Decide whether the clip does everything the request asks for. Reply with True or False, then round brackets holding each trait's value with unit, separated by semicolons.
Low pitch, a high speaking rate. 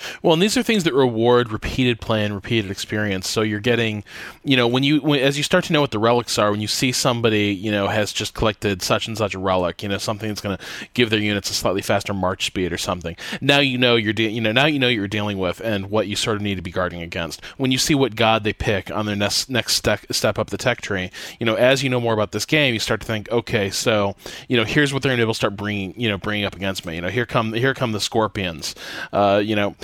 True (110 Hz; 285 wpm)